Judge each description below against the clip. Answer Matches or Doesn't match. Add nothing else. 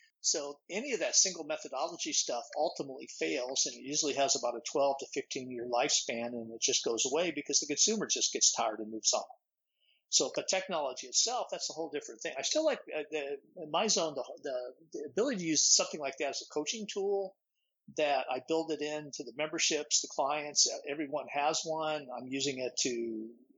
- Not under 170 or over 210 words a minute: Matches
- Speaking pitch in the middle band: Matches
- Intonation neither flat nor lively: Doesn't match